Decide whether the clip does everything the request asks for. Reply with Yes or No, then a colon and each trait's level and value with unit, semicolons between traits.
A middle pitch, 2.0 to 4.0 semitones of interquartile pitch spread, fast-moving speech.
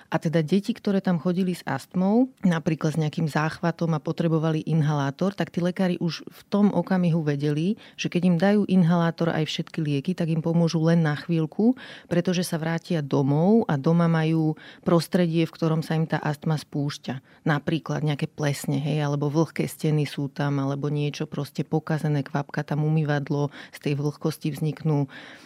Yes: medium, 160 Hz; narrow, 2.6 semitones; fast, 170 wpm